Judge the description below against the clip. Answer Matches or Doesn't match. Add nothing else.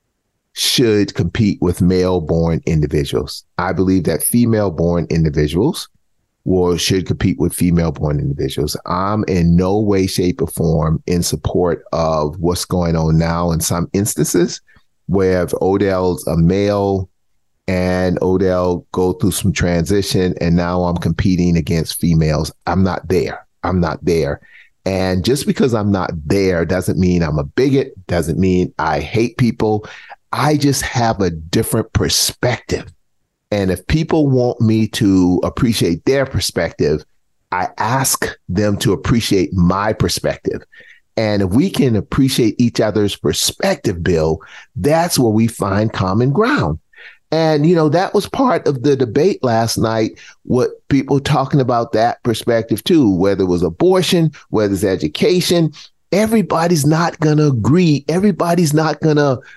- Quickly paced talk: Doesn't match